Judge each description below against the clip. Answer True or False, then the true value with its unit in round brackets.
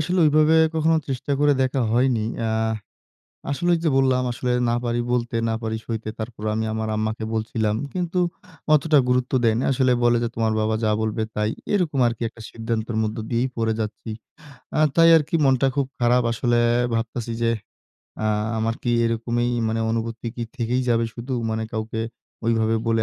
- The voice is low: True (115 Hz)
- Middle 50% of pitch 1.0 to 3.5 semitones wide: True (2.8 semitones)